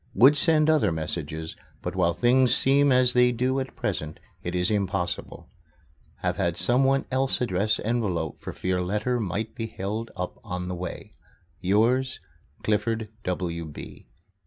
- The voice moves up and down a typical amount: No, wide, 5.9 semitones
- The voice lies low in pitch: Yes, low, 105 Hz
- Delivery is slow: No, average, 145 wpm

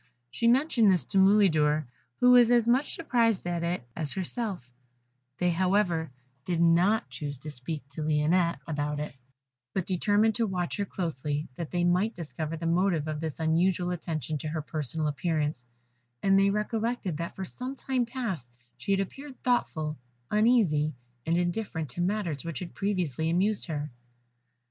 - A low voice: No, medium, 175 Hz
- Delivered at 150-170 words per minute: Yes, average, 165 wpm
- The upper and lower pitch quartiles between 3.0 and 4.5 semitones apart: No, average, 5.0 semitones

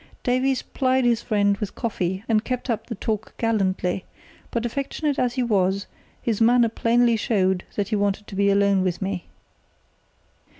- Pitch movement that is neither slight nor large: Yes, average, 3.4 semitones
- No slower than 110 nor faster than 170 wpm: Yes, average, 165 wpm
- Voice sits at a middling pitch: No, high, 215 Hz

